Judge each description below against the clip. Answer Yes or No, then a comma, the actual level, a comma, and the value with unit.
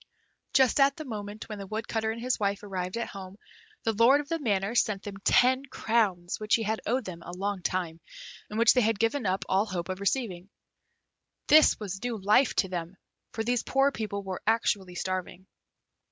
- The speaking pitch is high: Yes, high, 210 Hz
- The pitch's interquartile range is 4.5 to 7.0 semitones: No, average, 3.6 semitones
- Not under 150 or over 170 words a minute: No, average, 195 wpm